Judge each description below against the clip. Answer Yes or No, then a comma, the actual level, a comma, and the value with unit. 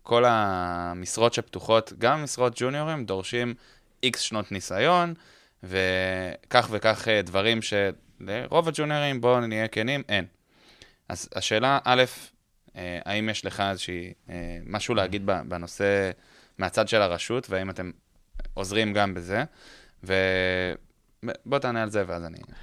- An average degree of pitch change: Yes, average, 4.6 semitones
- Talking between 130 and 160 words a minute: No, average, 115 wpm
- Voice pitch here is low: Yes, low, 105 Hz